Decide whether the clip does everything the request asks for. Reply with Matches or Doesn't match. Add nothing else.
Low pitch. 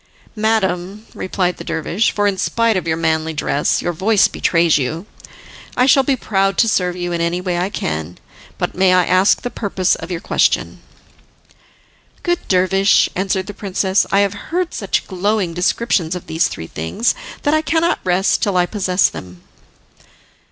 Doesn't match